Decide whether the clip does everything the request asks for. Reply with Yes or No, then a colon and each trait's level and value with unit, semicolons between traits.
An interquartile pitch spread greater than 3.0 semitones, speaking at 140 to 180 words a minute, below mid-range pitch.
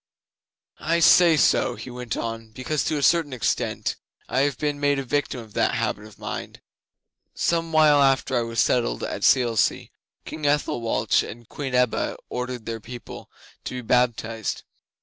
Yes: average, 3.9 semitones; average, 165 wpm; low, 125 Hz